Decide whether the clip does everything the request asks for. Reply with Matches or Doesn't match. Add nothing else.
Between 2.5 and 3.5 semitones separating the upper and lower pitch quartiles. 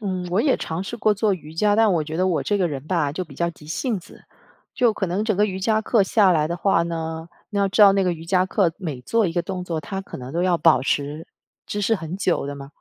Doesn't match